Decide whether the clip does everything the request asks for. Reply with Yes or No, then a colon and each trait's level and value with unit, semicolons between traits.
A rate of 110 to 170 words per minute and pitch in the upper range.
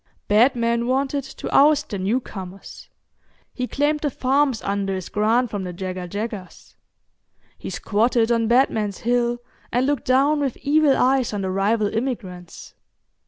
Yes: average, 145 wpm; high, 235 Hz